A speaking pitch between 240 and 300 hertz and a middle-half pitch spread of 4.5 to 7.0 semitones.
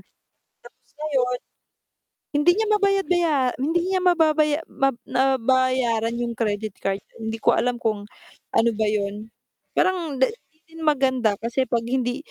Yes: very high, 260 Hz; average, 5.2 semitones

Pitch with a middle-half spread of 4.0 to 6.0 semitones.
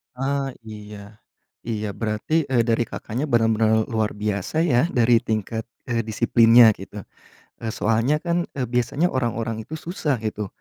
No: average, 3.2 semitones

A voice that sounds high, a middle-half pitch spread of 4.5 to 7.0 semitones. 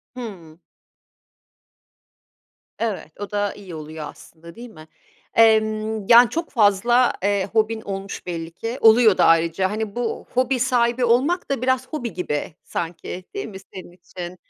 Yes: high, 215 Hz; average, 4.9 semitones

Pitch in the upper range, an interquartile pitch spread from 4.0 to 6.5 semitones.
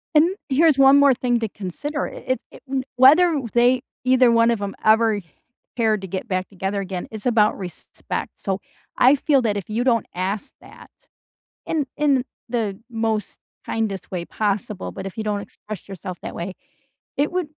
Yes: high, 225 Hz; average, 4.7 semitones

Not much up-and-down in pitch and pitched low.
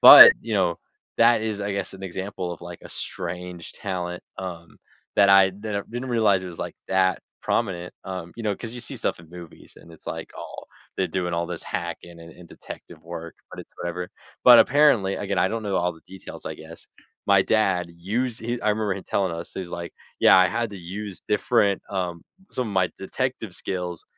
No: average, 3.1 semitones; very low, 95 Hz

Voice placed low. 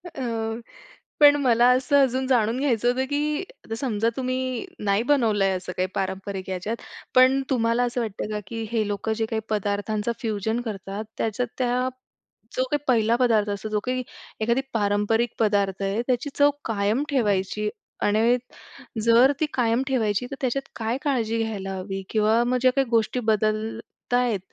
No: high, 225 Hz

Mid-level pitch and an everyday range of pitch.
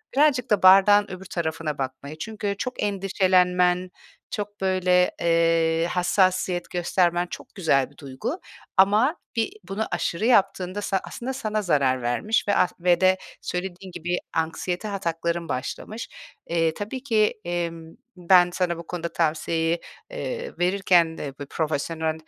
Yes: medium, 180 Hz; average, 3.3 semitones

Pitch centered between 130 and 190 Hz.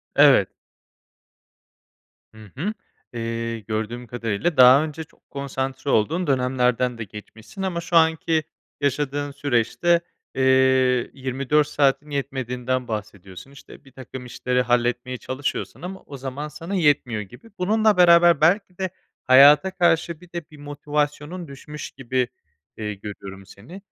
Yes: low, 135 Hz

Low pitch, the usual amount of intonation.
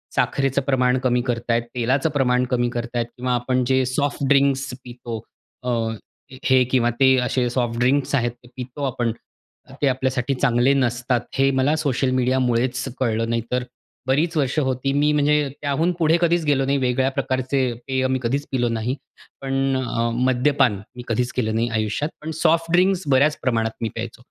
No: low, 130 Hz; narrow, 2.3 semitones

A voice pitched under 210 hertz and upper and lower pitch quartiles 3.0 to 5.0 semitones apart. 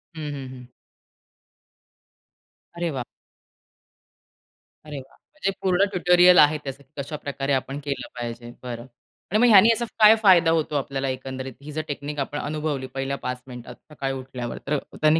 Yes: medium, 140 Hz; average, 3.4 semitones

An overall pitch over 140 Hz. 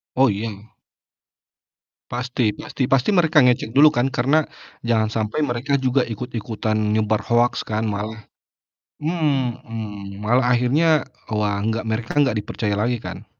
No: low, 120 Hz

